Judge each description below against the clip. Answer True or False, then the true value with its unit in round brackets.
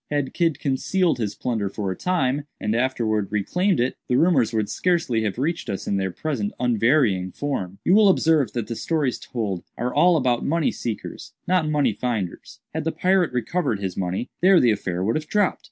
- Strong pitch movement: True (7.2 semitones)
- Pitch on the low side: True (125 Hz)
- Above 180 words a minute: True (200 wpm)